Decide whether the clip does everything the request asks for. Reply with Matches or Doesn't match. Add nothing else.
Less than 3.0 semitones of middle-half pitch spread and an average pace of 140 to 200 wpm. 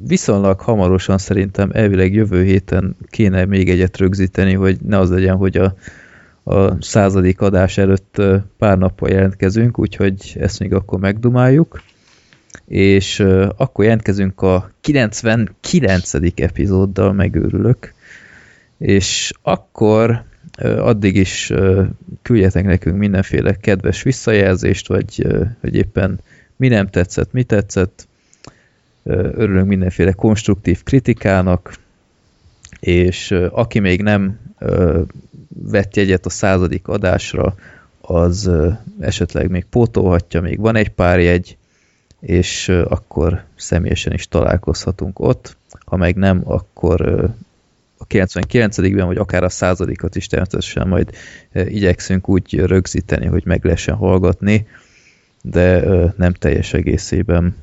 Doesn't match